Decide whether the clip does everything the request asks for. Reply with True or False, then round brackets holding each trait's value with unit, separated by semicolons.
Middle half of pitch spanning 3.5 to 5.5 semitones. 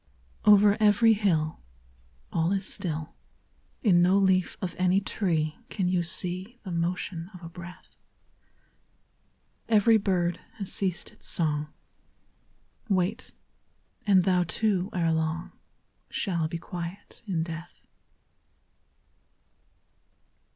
False (2.7 semitones)